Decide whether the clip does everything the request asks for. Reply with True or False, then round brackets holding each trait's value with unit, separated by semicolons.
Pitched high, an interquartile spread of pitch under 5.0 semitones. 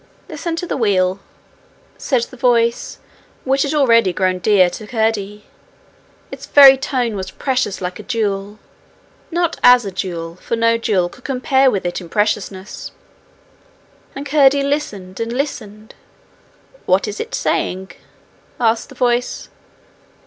False (230 Hz; 5.4 semitones)